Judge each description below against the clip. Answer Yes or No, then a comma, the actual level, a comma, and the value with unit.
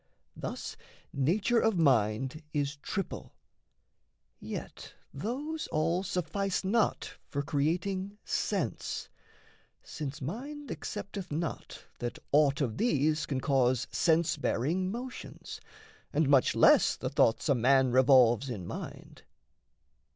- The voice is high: No, medium, 155 Hz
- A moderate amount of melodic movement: No, wide, 6.5 semitones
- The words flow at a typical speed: No, slow, 110 wpm